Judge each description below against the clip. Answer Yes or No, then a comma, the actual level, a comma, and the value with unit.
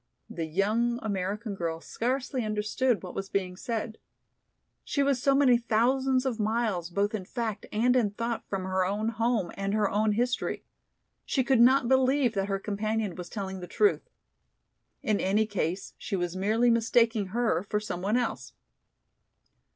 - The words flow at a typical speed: Yes, average, 165 wpm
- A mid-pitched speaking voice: No, high, 215 Hz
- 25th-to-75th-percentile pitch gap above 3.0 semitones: Yes, average, 3.5 semitones